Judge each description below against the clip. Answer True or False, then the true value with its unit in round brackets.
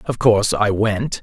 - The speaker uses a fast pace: False (195 wpm)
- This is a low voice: True (105 Hz)